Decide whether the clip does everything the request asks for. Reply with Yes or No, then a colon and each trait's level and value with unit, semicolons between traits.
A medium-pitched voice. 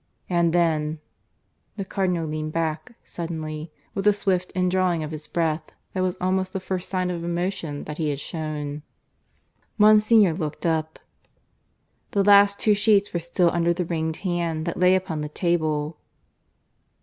Yes: medium, 170 Hz